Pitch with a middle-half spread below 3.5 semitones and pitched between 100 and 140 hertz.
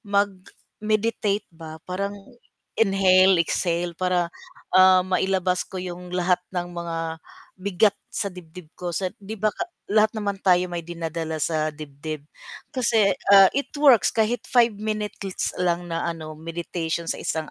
No: average, 3.0 semitones; medium, 185 Hz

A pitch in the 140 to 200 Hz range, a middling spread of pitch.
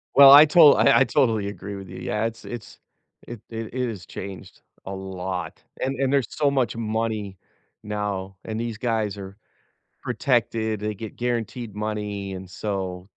No: low, 110 Hz; average, 3.3 semitones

